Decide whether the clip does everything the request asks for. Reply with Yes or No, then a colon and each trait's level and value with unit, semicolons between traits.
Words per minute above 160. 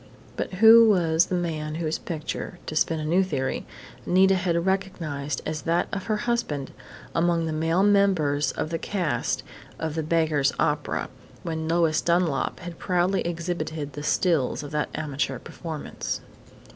No: average, 155 wpm